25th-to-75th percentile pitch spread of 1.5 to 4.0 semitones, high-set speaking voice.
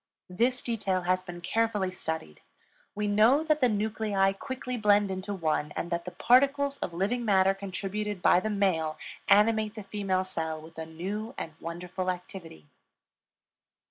Yes: average, 3.5 semitones; high, 195 Hz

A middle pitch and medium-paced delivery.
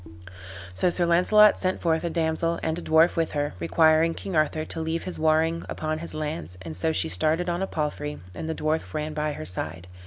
No: medium, 160 Hz; fast, 215 wpm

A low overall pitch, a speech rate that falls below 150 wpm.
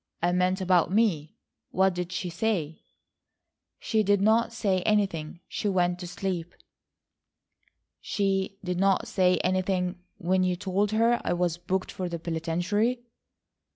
No: medium, 185 Hz; average, 140 wpm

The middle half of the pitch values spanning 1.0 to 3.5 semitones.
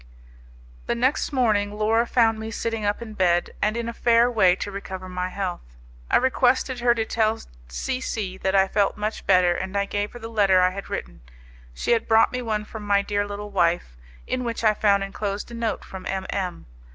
Yes: average, 3.0 semitones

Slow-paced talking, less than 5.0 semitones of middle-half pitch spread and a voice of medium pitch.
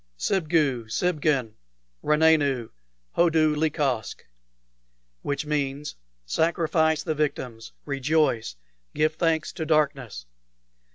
Yes: slow, 80 wpm; average, 2.8 semitones; medium, 150 Hz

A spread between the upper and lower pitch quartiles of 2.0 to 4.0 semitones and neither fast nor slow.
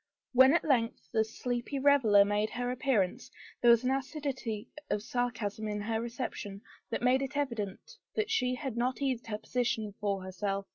Yes: average, 3.7 semitones; average, 175 wpm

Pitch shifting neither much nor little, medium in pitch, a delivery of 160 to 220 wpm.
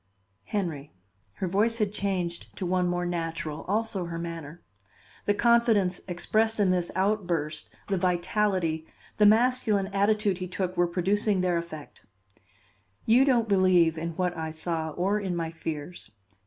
No: average, 3.4 semitones; medium, 180 Hz; average, 145 wpm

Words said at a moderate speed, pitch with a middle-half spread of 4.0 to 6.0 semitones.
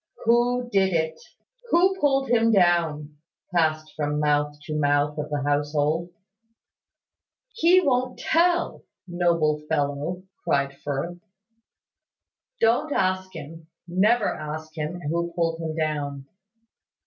No: slow, 115 wpm; average, 4.7 semitones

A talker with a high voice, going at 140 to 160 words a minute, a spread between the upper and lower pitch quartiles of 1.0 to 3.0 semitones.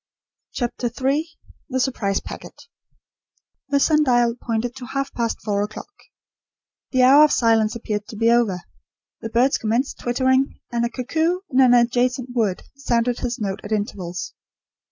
Yes: high, 240 Hz; average, 155 wpm; average, 2.7 semitones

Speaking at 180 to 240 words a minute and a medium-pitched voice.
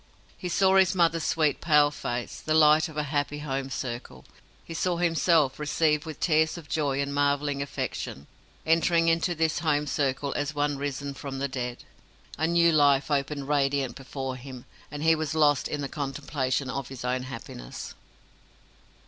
No: average, 170 wpm; medium, 145 Hz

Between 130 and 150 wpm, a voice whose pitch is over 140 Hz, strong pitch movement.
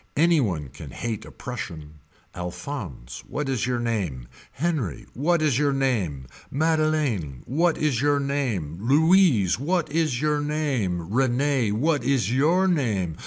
No: average, 140 wpm; low, 130 Hz; wide, 7.4 semitones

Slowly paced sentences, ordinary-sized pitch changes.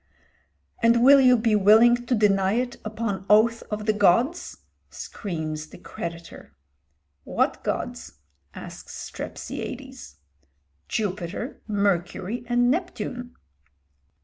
Yes: slow, 100 wpm; average, 4.0 semitones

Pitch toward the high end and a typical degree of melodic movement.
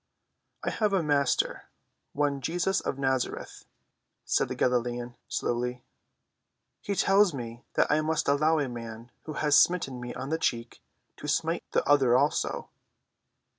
No: medium, 140 Hz; average, 4.2 semitones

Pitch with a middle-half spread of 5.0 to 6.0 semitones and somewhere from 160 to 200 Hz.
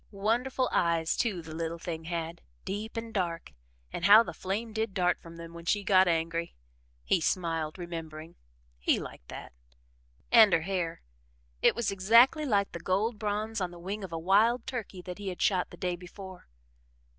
No: average, 4.0 semitones; medium, 185 Hz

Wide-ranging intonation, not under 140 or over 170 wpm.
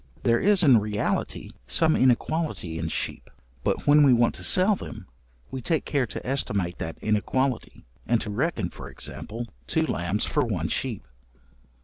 Yes: wide, 5.9 semitones; average, 160 wpm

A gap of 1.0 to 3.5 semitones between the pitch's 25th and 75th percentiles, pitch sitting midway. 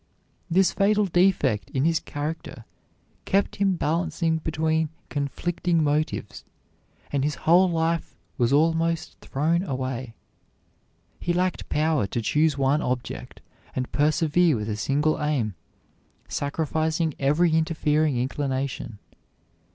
Yes: average, 3.1 semitones; medium, 155 Hz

